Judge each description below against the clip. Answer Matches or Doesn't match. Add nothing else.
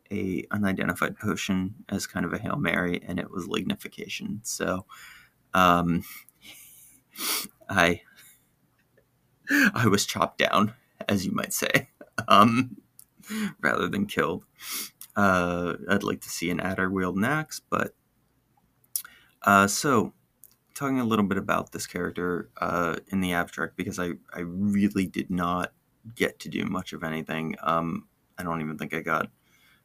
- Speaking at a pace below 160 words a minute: Matches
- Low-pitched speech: Matches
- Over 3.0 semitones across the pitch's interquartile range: Doesn't match